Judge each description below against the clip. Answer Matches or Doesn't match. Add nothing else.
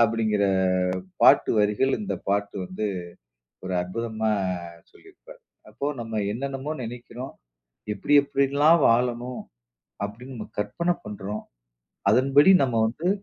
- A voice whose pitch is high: Doesn't match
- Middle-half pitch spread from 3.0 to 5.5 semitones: Matches